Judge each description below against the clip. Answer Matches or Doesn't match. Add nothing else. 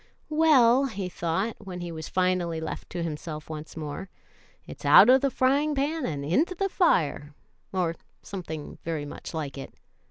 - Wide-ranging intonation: Matches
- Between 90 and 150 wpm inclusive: Doesn't match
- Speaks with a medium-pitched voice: Matches